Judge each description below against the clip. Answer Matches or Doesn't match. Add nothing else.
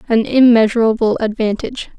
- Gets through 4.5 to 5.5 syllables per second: Doesn't match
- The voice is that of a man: Doesn't match